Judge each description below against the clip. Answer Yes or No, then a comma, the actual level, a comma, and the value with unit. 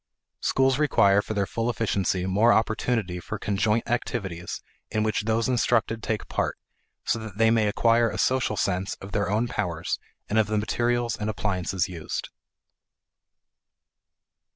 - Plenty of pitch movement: No, average, 2.8 semitones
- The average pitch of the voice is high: No, low, 110 Hz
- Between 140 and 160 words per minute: Yes, average, 150 wpm